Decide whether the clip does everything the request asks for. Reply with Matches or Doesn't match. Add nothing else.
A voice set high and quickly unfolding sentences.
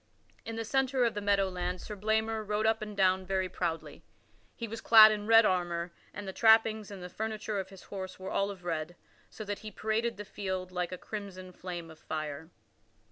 Matches